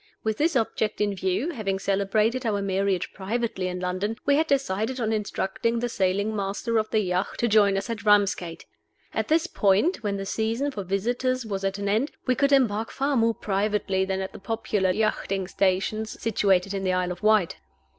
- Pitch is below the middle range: No, high, 210 Hz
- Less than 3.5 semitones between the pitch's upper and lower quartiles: Yes, average, 3.0 semitones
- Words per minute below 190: No, average, 195 wpm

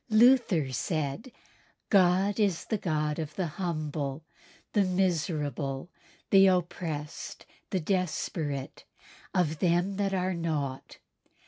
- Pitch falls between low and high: Yes, medium, 170 Hz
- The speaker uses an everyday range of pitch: Yes, average, 4.0 semitones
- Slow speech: Yes, slow, 105 wpm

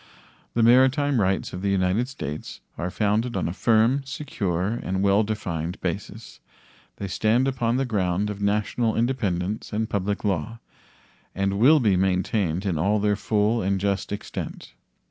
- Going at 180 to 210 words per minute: No, average, 155 wpm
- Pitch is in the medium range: No, low, 105 Hz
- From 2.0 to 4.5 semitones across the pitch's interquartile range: Yes, average, 3.5 semitones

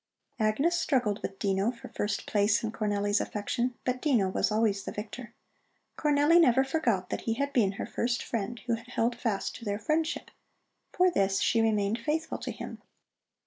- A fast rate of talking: No, average, 180 wpm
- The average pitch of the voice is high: Yes, high, 230 Hz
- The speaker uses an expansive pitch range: No, average, 4.0 semitones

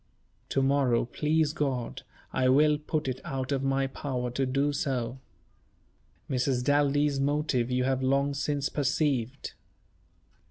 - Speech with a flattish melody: Yes, narrow, 2.0 semitones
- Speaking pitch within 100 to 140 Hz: Yes, low, 135 Hz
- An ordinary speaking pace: No, slow, 130 wpm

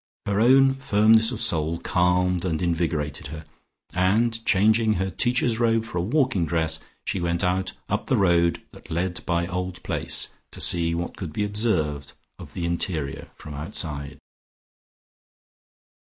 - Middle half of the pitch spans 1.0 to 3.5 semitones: No, average, 4.5 semitones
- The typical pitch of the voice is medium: No, very low, 90 Hz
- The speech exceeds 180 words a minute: No, average, 150 wpm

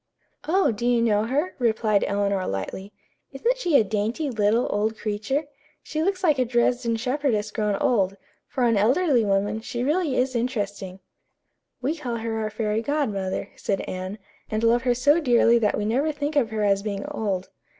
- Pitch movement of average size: Yes, average, 4.2 semitones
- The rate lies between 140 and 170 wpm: No, average, 180 wpm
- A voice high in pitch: Yes, high, 230 Hz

